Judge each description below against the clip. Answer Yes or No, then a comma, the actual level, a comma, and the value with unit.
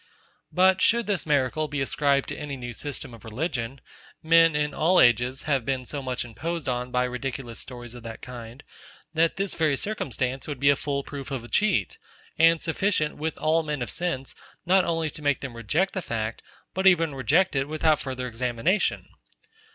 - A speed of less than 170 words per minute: No, average, 190 wpm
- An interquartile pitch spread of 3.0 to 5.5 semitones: Yes, average, 4.6 semitones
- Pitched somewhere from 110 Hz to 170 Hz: Yes, medium, 140 Hz